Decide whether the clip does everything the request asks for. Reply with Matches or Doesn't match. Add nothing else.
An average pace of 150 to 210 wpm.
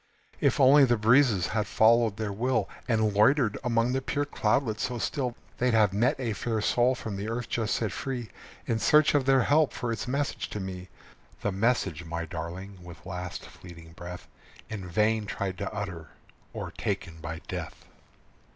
Matches